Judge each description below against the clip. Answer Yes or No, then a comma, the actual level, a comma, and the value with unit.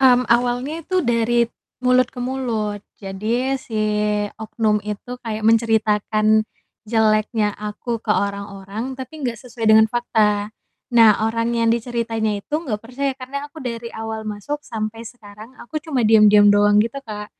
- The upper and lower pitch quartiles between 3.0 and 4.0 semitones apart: No, narrow, 2.5 semitones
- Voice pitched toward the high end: Yes, high, 225 Hz